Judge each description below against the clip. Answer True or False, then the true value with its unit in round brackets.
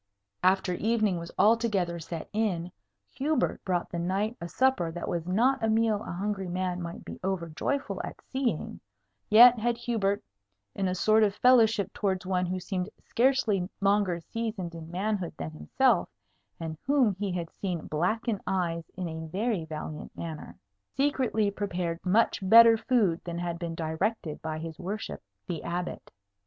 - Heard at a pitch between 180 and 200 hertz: True (190 Hz)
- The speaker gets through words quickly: False (160 wpm)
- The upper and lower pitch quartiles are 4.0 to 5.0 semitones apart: True (4.4 semitones)